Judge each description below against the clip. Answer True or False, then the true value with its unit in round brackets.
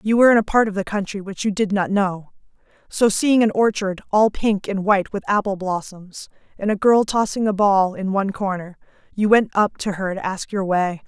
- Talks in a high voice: True (200 Hz)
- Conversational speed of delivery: False (225 wpm)